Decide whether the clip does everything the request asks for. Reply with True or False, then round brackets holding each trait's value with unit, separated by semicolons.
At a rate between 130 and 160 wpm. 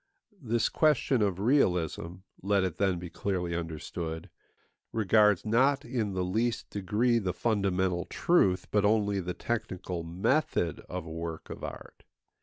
True (140 wpm)